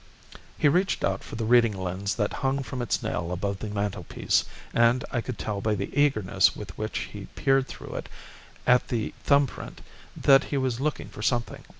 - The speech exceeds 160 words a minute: Yes, average, 195 wpm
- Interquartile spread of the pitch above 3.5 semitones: Yes, average, 4.7 semitones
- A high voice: No, low, 115 Hz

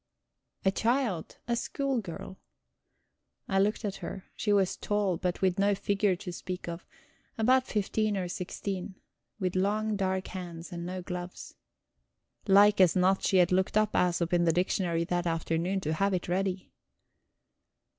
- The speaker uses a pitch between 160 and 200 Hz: Yes, high, 190 Hz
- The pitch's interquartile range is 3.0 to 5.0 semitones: No, narrow, 2.5 semitones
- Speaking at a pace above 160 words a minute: No, average, 155 wpm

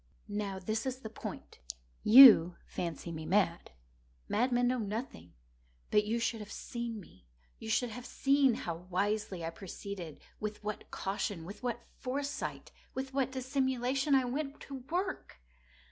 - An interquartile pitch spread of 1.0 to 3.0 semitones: No, average, 5.1 semitones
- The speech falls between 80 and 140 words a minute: Yes, slow, 135 wpm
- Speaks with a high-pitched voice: Yes, high, 225 Hz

